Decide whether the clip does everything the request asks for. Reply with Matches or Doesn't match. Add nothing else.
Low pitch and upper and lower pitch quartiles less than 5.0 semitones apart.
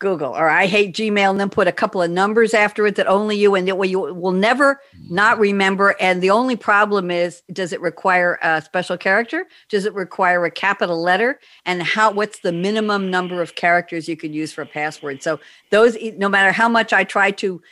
Doesn't match